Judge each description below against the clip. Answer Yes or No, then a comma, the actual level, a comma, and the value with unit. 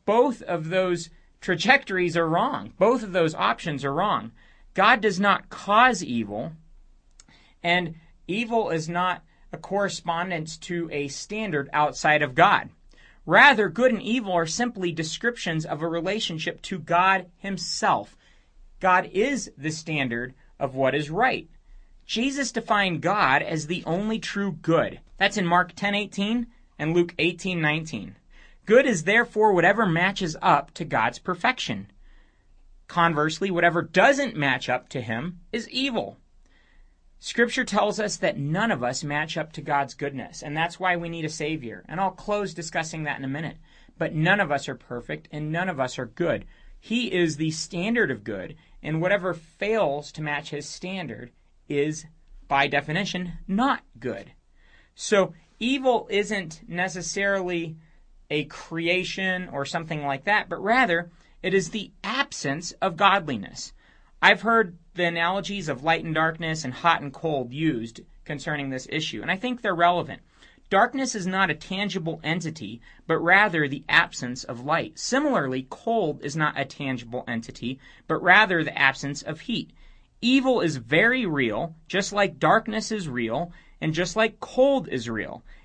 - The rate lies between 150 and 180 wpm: Yes, average, 155 wpm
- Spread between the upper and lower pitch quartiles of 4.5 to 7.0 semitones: Yes, average, 5.0 semitones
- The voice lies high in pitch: No, medium, 170 Hz